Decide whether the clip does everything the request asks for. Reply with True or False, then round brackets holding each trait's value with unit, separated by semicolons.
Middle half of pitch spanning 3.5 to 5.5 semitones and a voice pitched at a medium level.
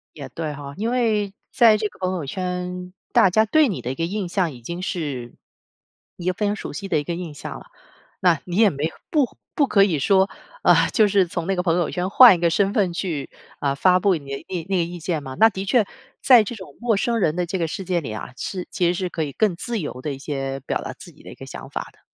True (4.1 semitones; 180 Hz)